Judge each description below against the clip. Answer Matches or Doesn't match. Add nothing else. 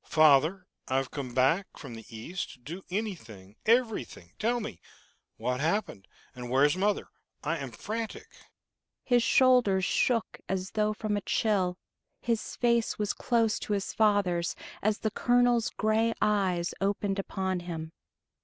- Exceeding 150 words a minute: Doesn't match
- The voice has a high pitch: Matches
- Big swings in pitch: Matches